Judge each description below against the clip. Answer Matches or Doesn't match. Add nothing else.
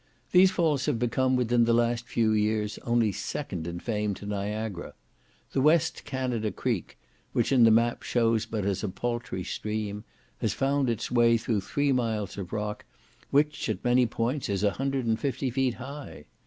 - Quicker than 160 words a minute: Matches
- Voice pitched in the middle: Doesn't match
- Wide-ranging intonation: Doesn't match